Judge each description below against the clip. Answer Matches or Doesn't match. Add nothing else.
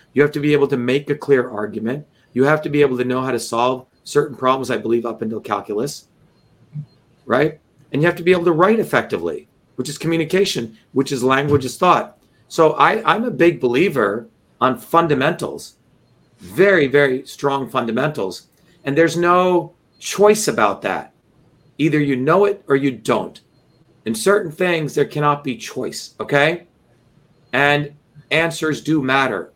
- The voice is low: Doesn't match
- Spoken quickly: Doesn't match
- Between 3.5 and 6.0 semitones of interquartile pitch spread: Matches